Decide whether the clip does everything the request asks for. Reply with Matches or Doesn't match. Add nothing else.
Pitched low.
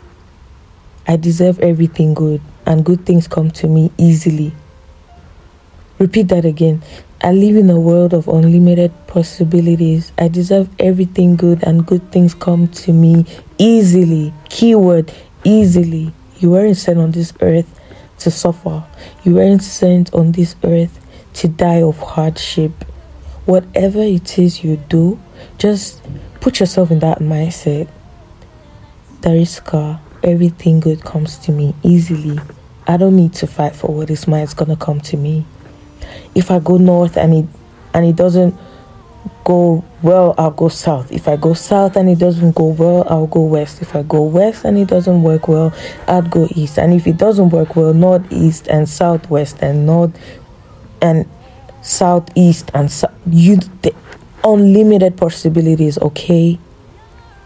Doesn't match